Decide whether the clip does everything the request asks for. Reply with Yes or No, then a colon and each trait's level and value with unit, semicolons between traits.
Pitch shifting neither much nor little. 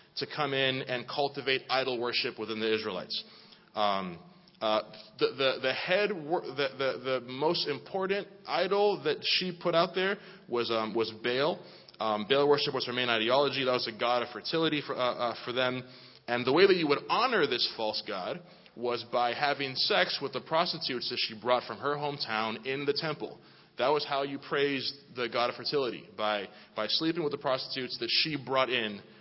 Yes: average, 4.2 semitones